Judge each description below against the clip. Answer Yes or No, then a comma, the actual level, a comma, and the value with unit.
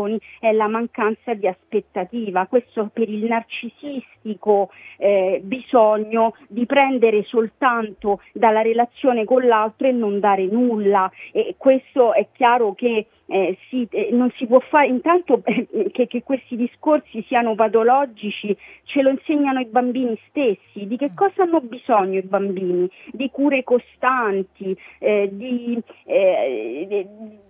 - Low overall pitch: No, high, 235 Hz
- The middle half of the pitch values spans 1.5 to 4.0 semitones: Yes, average, 3.6 semitones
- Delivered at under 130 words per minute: No, average, 135 wpm